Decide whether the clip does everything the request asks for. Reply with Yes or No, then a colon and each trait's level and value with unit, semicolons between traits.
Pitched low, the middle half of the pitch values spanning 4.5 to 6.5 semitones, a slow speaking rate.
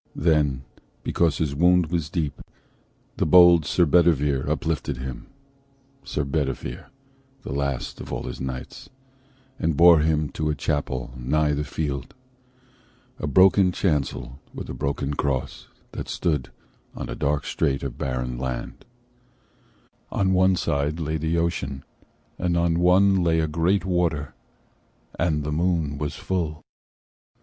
No: very low, 75 Hz; average, 3.7 semitones; slow, 120 wpm